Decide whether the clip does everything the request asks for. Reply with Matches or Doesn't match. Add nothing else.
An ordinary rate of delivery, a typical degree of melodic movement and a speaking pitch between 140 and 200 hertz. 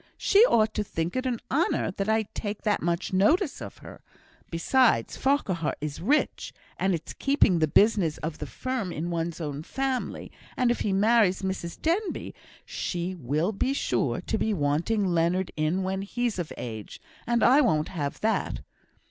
Doesn't match